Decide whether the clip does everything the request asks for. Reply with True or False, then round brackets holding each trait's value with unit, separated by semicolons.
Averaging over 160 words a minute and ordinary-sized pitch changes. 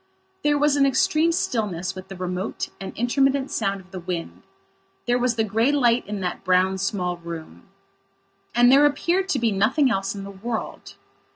False (180 wpm; 6.1 semitones)